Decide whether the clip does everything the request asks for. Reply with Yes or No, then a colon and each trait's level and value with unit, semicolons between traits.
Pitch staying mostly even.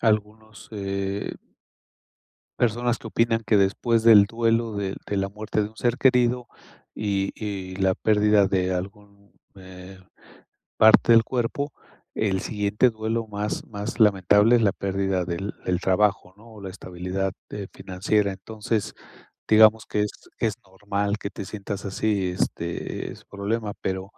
Yes: narrow, 2.2 semitones